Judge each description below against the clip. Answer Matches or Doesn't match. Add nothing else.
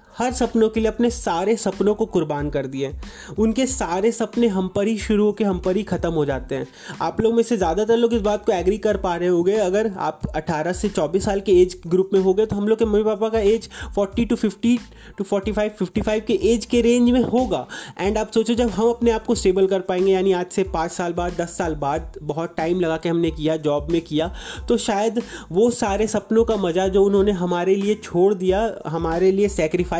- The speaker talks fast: Matches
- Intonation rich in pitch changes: Doesn't match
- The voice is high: Matches